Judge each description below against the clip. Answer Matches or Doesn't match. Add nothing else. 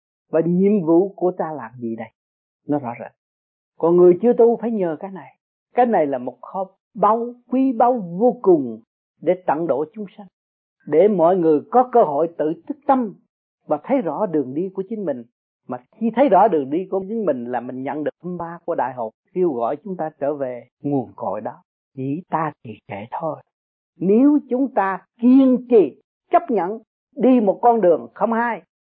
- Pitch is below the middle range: Doesn't match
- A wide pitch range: Matches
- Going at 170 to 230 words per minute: Matches